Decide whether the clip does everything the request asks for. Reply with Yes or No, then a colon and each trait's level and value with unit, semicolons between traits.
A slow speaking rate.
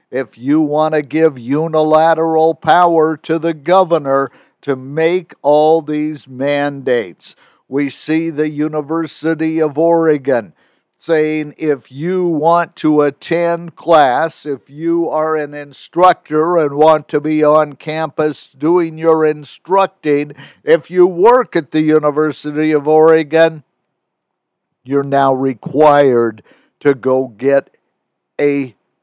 Yes: slow, 120 wpm